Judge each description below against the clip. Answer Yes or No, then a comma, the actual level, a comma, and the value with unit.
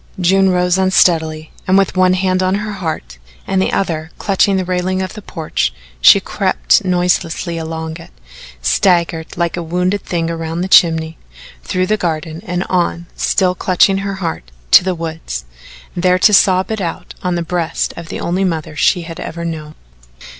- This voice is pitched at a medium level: Yes, medium, 175 Hz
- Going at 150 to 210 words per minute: Yes, average, 175 wpm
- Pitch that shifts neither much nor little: No, narrow, 2.3 semitones